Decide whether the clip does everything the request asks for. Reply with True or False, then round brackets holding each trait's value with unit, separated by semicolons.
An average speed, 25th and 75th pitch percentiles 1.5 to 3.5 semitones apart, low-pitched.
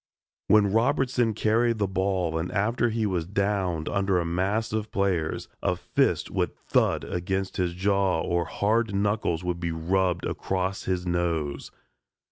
True (150 wpm; 3.1 semitones; 95 Hz)